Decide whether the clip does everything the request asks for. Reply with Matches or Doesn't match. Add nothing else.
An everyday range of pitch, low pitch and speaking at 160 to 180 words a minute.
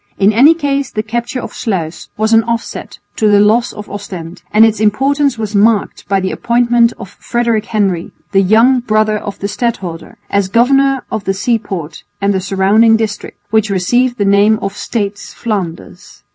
Doesn't match